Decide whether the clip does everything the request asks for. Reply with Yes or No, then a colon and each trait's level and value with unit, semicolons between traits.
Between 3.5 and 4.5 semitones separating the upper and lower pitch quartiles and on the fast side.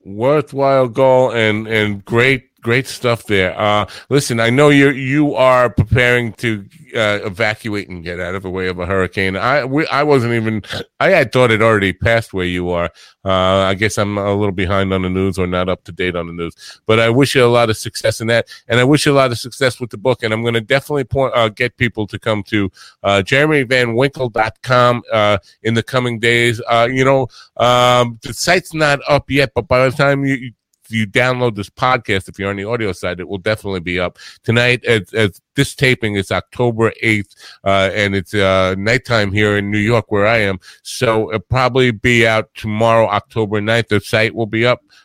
Yes: average, 3.8 semitones; fast, 215 wpm